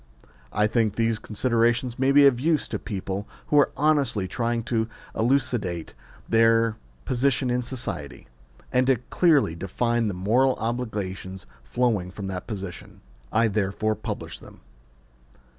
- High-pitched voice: No, low, 115 Hz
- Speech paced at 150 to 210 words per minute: No, slow, 135 wpm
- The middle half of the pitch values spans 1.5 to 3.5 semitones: No, average, 3.9 semitones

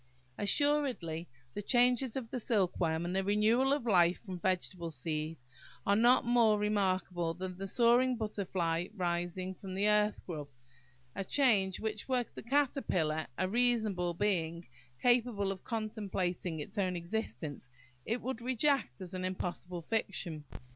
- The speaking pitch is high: Yes, high, 195 Hz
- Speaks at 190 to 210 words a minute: No, average, 140 wpm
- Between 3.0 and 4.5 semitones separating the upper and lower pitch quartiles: No, average, 4.9 semitones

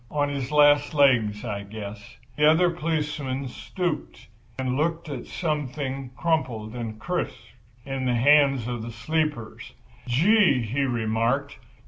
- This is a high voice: No, low, 135 Hz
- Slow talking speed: Yes, slow, 130 wpm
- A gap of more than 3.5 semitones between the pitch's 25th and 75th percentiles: Yes, average, 4.3 semitones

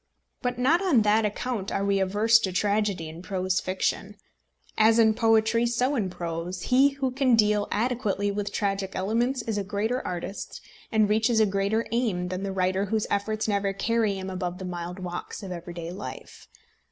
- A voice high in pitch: Yes, high, 205 Hz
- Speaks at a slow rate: No, average, 180 wpm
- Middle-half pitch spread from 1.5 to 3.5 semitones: Yes, average, 3.2 semitones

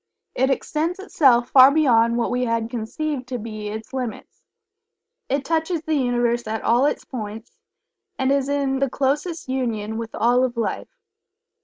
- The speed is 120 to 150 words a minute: No, average, 160 wpm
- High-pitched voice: Yes, very high, 255 Hz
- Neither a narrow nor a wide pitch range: Yes, average, 3.3 semitones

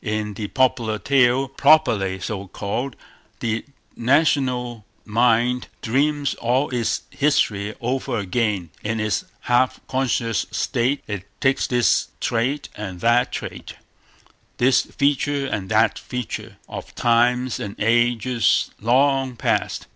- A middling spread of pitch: Yes, average, 3.3 semitones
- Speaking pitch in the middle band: No, low, 120 Hz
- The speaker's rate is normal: No, slow, 115 wpm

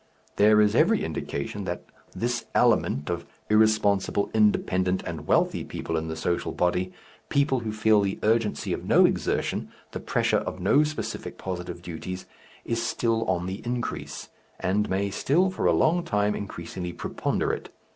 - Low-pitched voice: Yes, low, 100 Hz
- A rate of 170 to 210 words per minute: No, average, 155 wpm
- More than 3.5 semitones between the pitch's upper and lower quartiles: Yes, average, 3.9 semitones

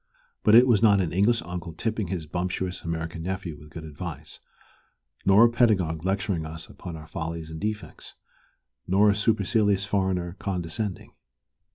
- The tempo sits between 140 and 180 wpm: Yes, average, 155 wpm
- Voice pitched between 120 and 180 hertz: No, very low, 90 Hz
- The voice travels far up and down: No, average, 3.8 semitones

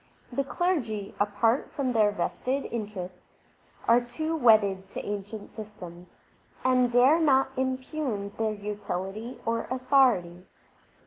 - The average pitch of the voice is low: No, high, 230 Hz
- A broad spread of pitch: No, average, 4.1 semitones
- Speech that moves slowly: Yes, slow, 115 wpm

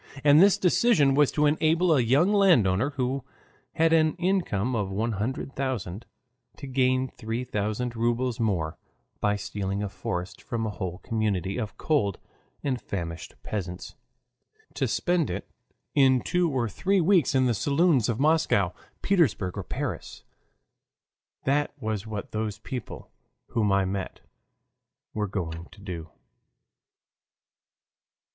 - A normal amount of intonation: No, wide, 6.6 semitones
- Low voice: Yes, low, 120 Hz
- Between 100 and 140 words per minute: Yes, slow, 135 wpm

